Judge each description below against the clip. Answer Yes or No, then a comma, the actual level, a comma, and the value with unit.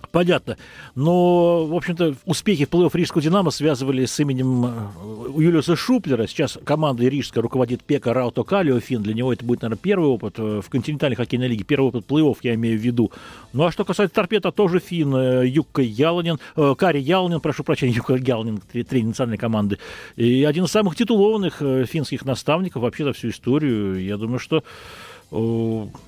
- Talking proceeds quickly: Yes, fast, 170 wpm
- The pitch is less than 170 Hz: Yes, low, 135 Hz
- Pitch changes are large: Yes, wide, 5.7 semitones